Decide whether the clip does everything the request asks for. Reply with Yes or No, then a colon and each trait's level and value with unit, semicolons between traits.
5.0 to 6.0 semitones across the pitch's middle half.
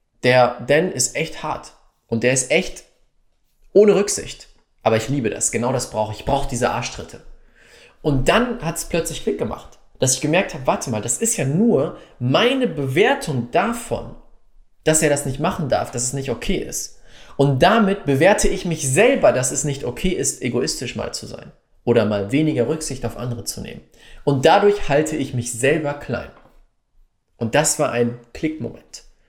Yes: wide, 5.5 semitones